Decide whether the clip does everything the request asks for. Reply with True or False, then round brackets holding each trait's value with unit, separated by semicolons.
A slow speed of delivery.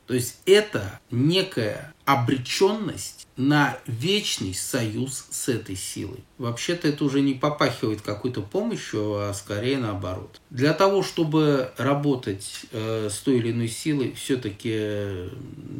False (125 wpm)